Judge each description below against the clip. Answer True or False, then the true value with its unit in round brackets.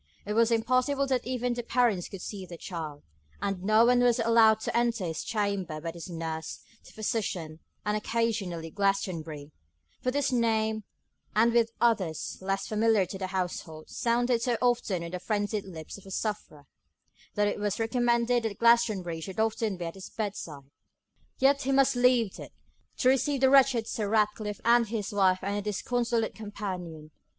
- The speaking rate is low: False (170 wpm)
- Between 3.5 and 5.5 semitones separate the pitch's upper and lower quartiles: True (4.1 semitones)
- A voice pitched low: False (215 Hz)